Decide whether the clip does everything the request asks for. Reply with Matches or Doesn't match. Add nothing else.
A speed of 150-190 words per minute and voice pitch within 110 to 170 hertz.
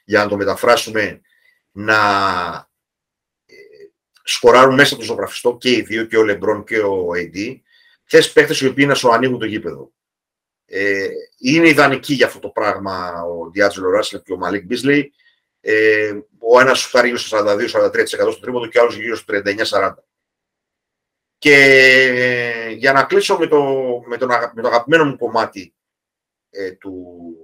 Matches